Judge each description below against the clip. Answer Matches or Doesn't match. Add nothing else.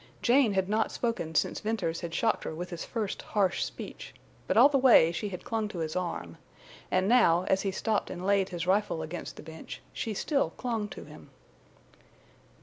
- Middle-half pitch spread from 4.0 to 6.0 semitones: Matches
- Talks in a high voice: Matches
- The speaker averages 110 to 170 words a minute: Doesn't match